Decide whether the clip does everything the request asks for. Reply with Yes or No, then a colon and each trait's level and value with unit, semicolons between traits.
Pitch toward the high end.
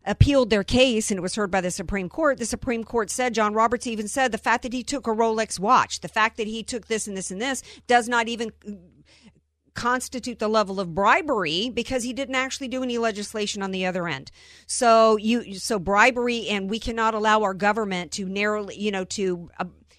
Yes: high, 220 Hz